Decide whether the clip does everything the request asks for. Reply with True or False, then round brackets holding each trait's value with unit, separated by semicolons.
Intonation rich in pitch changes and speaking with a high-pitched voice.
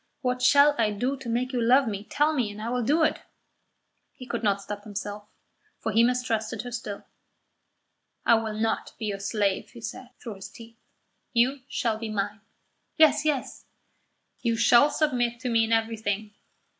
False (2.8 semitones; 230 Hz)